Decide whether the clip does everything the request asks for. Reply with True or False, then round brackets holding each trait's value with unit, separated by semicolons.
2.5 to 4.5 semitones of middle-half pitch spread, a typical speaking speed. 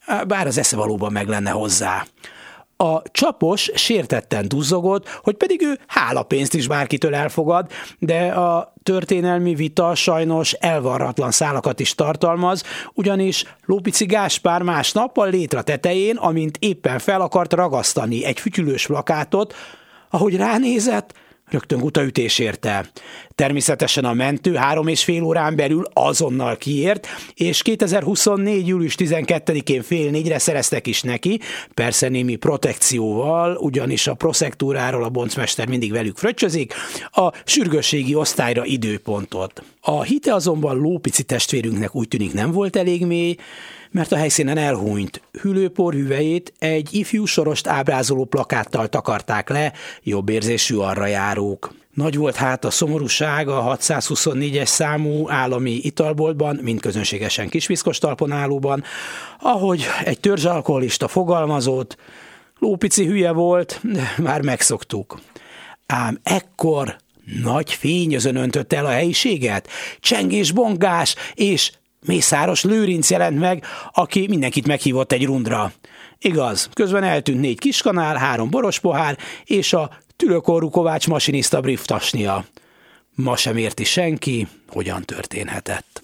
False (5.4 semitones; 120 wpm)